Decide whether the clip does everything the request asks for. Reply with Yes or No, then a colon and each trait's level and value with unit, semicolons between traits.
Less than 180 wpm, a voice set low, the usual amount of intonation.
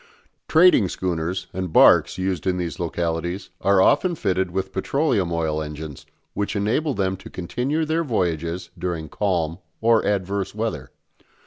Yes: average, 140 wpm; very low, 95 Hz; average, 3.6 semitones